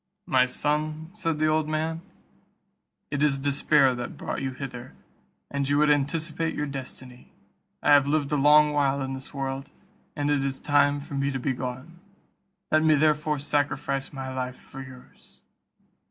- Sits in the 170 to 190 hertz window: No, medium, 145 Hz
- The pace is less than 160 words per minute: No, average, 170 wpm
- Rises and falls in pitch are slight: Yes, narrow, 2.1 semitones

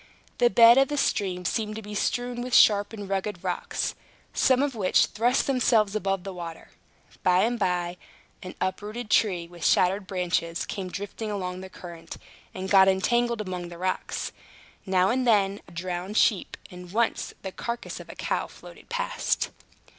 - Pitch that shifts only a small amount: No, average, 4.1 semitones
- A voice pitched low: No, high, 195 Hz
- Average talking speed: Yes, average, 170 wpm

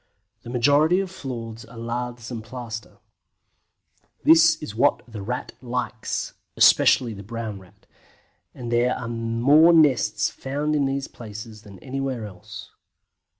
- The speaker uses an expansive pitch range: No, average, 3.6 semitones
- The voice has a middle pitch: No, low, 120 Hz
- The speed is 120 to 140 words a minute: Yes, slow, 135 wpm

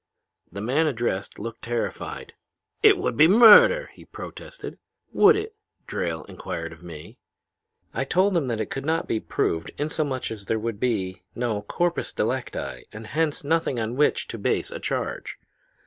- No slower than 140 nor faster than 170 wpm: Yes, average, 165 wpm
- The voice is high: No, low, 125 Hz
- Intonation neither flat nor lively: No, wide, 7.3 semitones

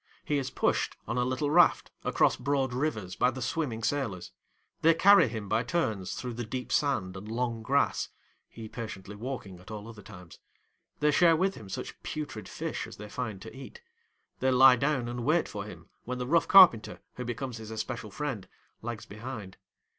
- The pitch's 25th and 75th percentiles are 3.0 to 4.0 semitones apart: No, average, 4.4 semitones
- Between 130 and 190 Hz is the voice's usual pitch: No, low, 120 Hz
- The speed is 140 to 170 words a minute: No, average, 190 wpm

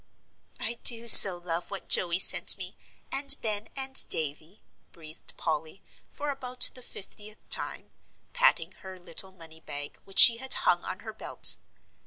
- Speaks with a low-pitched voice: No, high, 195 Hz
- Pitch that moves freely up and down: Yes, wide, 5.9 semitones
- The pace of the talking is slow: No, average, 155 wpm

